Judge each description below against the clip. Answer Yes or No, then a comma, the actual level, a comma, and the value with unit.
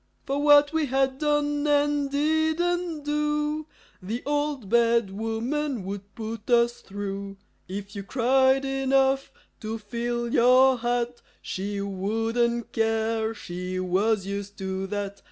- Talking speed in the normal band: No, slow, 125 wpm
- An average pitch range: No, wide, 5.9 semitones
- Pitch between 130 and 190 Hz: No, high, 235 Hz